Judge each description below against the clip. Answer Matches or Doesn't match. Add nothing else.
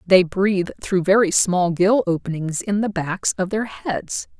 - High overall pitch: Doesn't match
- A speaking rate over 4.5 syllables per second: Doesn't match